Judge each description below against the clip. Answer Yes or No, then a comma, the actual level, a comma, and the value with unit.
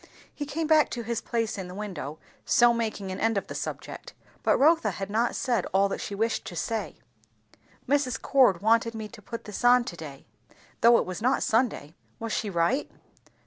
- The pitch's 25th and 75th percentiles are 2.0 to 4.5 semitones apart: Yes, average, 3.6 semitones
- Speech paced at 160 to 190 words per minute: No, average, 200 wpm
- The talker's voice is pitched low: No, high, 225 Hz